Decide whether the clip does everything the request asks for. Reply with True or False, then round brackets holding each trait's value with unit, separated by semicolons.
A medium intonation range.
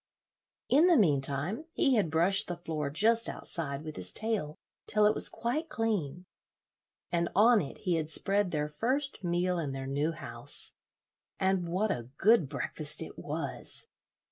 False (6.3 semitones)